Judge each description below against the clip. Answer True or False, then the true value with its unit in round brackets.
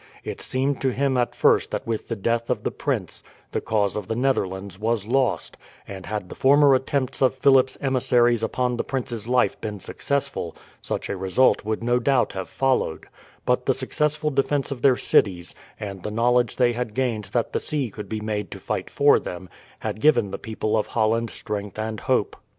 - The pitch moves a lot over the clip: False (3.8 semitones)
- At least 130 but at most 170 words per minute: False (195 wpm)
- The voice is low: True (120 Hz)